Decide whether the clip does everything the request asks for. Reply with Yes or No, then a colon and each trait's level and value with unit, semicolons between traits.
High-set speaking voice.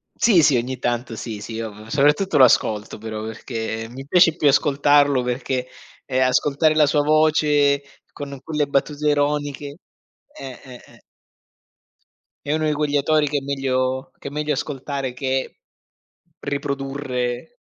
No: medium, 140 Hz